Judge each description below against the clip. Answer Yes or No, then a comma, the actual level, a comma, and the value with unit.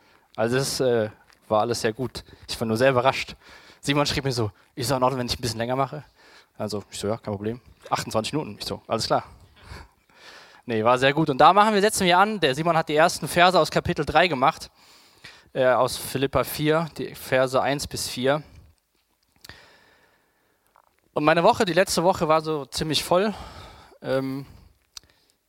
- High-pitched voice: No, low, 135 Hz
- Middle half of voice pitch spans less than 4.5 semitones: No, wide, 5.5 semitones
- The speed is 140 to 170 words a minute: No, average, 185 wpm